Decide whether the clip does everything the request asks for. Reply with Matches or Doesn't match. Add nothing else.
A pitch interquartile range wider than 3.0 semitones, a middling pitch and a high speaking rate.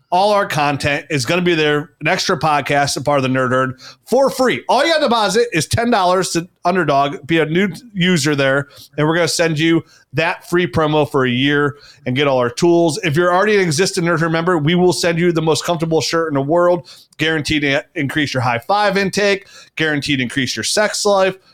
Matches